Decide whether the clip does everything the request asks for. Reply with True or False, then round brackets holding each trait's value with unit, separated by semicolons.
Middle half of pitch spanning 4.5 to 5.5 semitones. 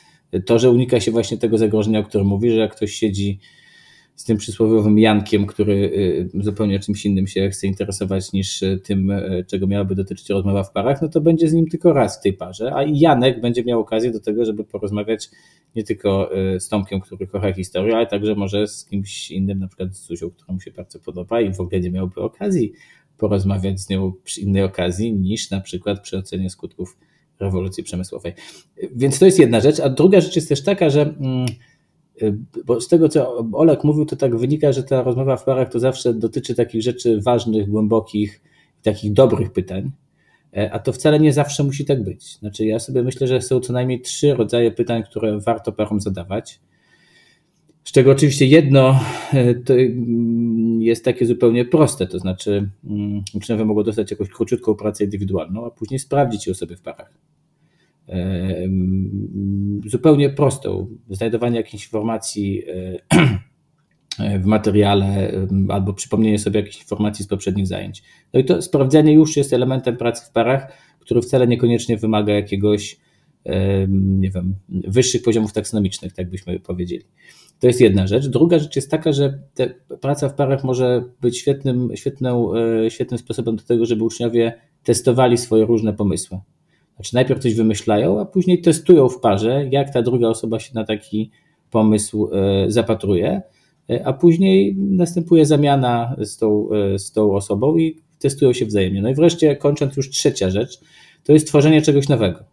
True (4.8 semitones)